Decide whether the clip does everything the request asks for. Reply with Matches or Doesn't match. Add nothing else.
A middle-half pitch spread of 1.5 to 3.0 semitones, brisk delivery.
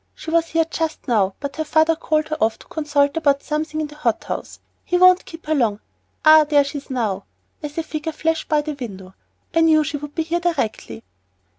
Matches